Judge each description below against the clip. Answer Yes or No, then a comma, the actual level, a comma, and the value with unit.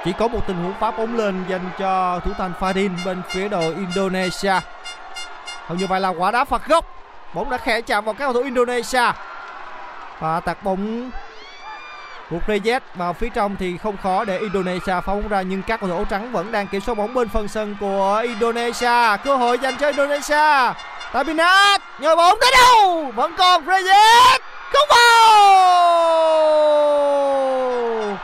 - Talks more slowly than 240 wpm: Yes, average, 170 wpm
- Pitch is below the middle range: No, high, 225 Hz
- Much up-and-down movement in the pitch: Yes, wide, 7.3 semitones